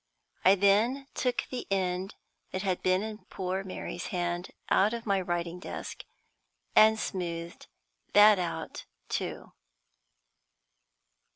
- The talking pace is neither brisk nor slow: No, slow, 115 wpm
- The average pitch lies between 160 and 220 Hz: Yes, high, 190 Hz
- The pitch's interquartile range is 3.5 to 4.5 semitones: No, average, 2.9 semitones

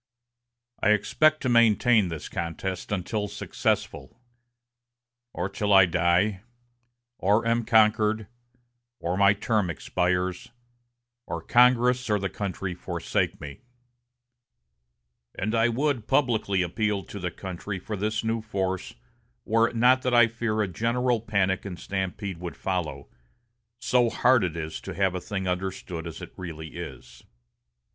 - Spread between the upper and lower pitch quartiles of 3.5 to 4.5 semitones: Yes, average, 3.9 semitones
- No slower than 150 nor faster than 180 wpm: No, slow, 135 wpm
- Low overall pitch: Yes, low, 100 Hz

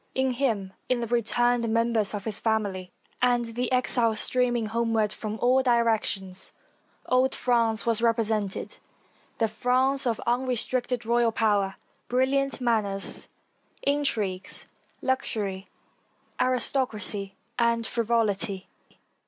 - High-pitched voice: Yes, high, 230 Hz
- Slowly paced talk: Yes, slow, 110 wpm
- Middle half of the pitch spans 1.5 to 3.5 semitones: Yes, average, 2.7 semitones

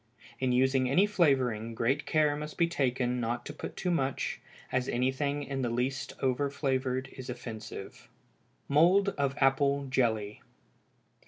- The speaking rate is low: No, average, 145 wpm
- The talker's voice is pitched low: Yes, low, 130 Hz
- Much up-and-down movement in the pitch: No, narrow, 2.5 semitones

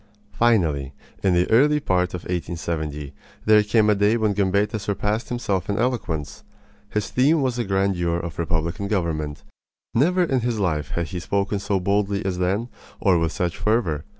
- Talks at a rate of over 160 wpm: Yes, average, 170 wpm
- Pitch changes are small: No, average, 4.2 semitones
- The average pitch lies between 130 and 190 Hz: No, low, 100 Hz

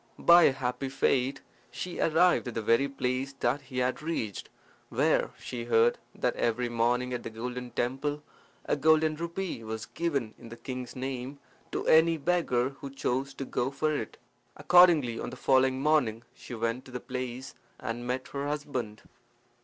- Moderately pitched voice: No, low, 130 Hz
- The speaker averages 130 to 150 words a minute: No, average, 170 wpm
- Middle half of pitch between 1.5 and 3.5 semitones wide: Yes, average, 3.2 semitones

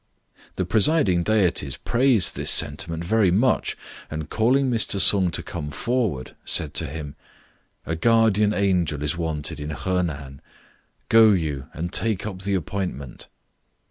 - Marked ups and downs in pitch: Yes, wide, 5.9 semitones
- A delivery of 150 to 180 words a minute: No, average, 140 wpm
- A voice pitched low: Yes, very low, 90 Hz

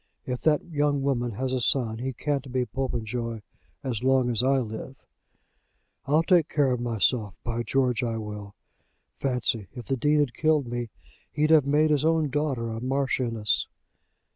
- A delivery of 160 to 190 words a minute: Yes, average, 165 wpm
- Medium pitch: No, low, 130 Hz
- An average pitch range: Yes, average, 3.5 semitones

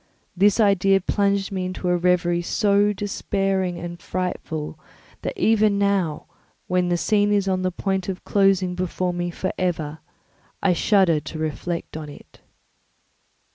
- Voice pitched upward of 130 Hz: Yes, medium, 185 Hz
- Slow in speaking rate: No, average, 145 wpm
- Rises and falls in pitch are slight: Yes, narrow, 2.3 semitones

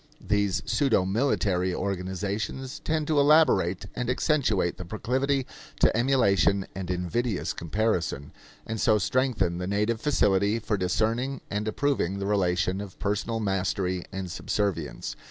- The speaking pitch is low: Yes, low, 100 Hz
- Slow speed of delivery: Yes, slow, 130 wpm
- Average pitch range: Yes, average, 4.6 semitones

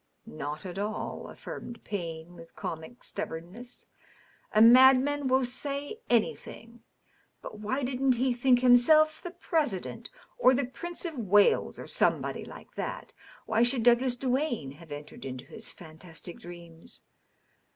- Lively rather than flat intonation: Yes, wide, 7.0 semitones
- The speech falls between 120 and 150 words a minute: Yes, average, 140 wpm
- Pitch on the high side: Yes, high, 240 Hz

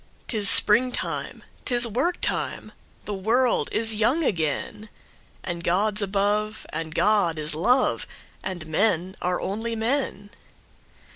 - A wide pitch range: No, average, 4.1 semitones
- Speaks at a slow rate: Yes, slow, 100 wpm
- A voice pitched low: No, high, 210 Hz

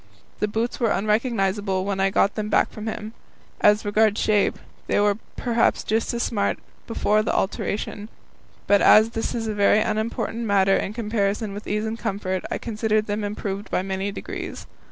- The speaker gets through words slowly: No, average, 175 wpm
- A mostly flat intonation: Yes, narrow, 1.7 semitones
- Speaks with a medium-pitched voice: No, high, 210 Hz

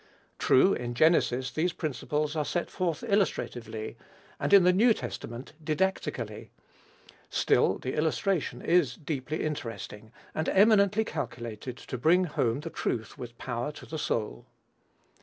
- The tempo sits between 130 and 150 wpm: Yes, slow, 135 wpm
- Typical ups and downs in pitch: No, wide, 6.6 semitones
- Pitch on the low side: No, medium, 150 Hz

